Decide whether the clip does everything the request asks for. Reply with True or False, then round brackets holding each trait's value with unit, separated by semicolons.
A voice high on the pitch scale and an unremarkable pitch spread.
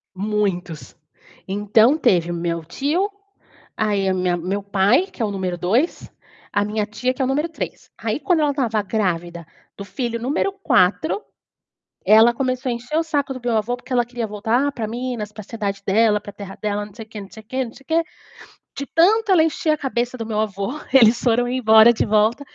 True (225 Hz; 4.2 semitones)